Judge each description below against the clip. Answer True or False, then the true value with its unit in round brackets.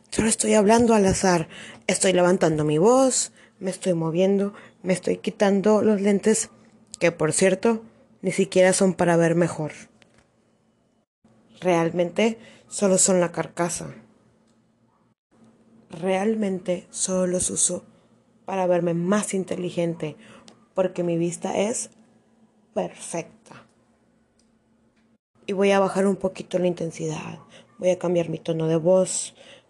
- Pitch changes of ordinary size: True (3.0 semitones)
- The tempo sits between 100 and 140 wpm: True (120 wpm)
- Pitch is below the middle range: False (185 Hz)